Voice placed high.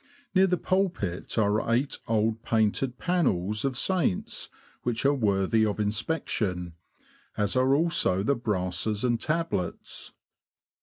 No: low, 115 Hz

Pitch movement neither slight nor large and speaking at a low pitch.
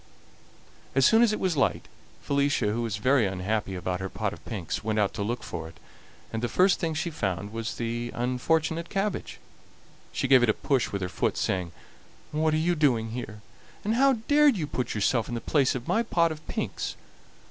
No: wide, 7.1 semitones; low, 125 Hz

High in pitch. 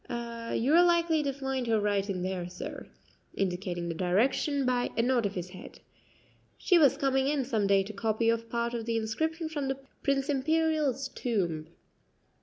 Yes: high, 235 Hz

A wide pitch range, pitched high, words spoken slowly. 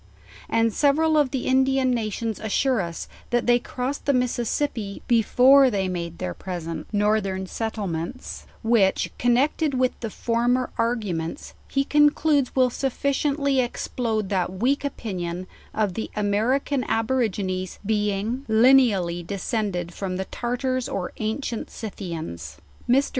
No: average, 5.0 semitones; high, 230 Hz; slow, 130 wpm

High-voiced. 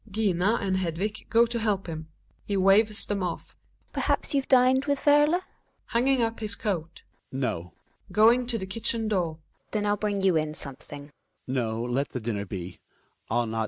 Yes: high, 205 Hz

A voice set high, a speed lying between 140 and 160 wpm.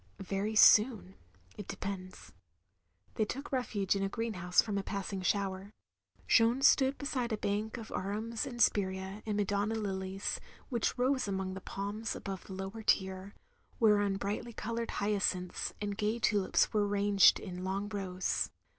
Yes: high, 205 Hz; average, 155 wpm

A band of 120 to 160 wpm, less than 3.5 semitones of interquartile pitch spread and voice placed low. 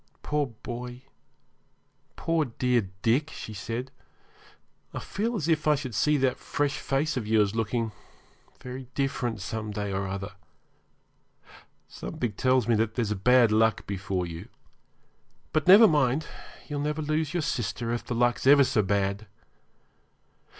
No: average, 145 wpm; average, 5.1 semitones; low, 125 Hz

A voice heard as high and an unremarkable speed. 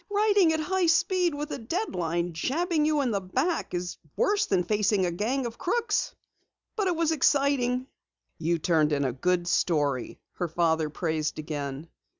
Yes: high, 210 Hz; average, 165 wpm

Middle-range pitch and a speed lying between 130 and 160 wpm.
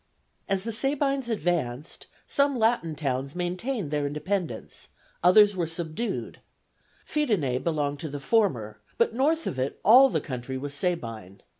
Yes: medium, 170 Hz; average, 140 wpm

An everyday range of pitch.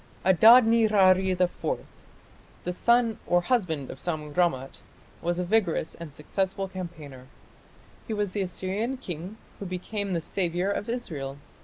Yes: average, 3.8 semitones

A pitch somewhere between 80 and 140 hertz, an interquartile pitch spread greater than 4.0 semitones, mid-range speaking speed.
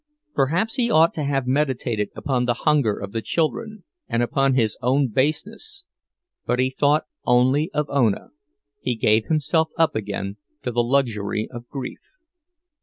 Yes: low, 135 Hz; average, 4.4 semitones; average, 155 wpm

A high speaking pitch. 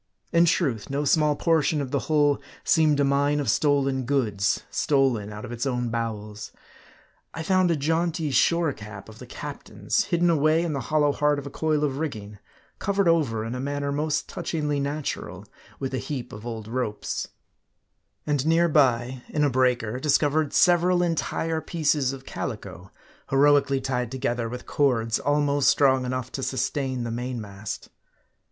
No: medium, 140 Hz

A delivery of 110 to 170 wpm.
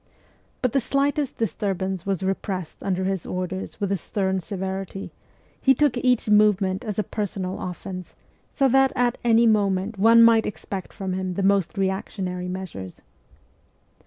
Yes: average, 150 wpm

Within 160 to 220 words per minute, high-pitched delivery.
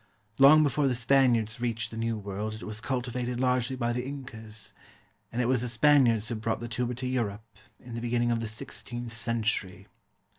No: average, 190 wpm; low, 120 Hz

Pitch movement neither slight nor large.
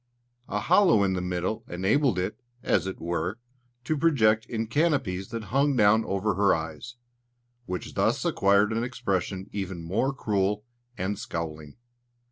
Yes: average, 3.8 semitones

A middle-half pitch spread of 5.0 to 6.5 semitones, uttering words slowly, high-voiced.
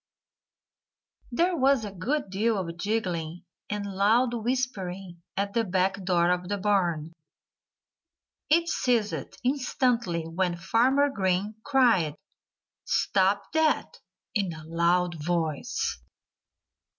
Yes: average, 5.3 semitones; slow, 105 wpm; high, 195 Hz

